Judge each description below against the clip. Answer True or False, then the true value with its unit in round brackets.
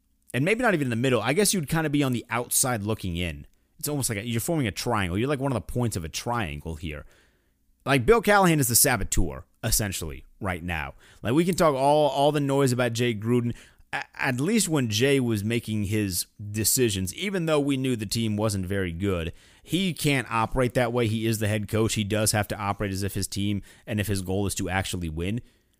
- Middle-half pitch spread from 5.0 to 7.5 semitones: True (5.6 semitones)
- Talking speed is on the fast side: True (235 wpm)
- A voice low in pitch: True (110 Hz)